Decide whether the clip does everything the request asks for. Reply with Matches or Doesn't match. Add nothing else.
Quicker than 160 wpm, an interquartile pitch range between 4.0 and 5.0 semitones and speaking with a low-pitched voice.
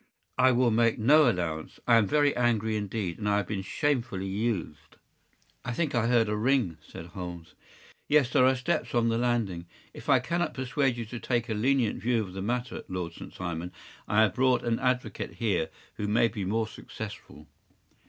Matches